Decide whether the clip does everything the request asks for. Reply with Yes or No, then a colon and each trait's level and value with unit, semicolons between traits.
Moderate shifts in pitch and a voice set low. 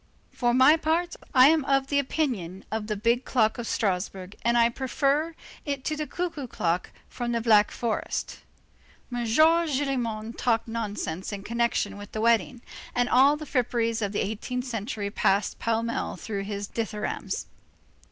No: average, 4.2 semitones; high, 235 Hz